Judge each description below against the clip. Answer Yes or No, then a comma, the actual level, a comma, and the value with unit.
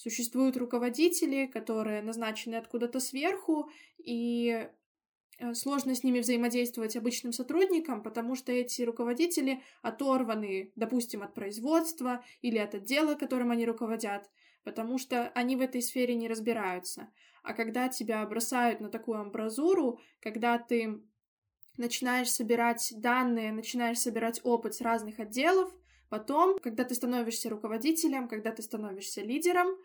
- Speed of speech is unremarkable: Yes, average, 125 wpm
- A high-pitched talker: Yes, high, 240 Hz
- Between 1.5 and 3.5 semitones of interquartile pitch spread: Yes, narrow, 2.5 semitones